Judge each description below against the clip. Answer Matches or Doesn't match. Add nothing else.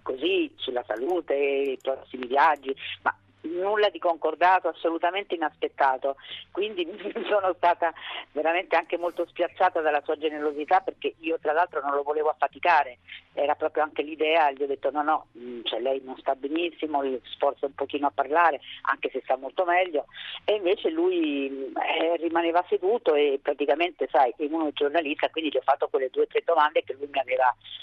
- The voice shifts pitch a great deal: Matches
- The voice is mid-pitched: Matches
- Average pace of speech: Doesn't match